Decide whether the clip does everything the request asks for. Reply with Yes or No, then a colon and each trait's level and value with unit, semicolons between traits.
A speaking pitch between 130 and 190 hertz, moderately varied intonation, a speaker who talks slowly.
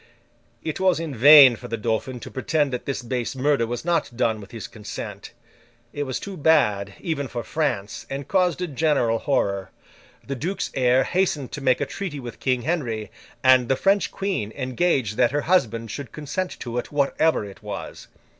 No: low, 135 Hz; average, 4.9 semitones; average, 185 wpm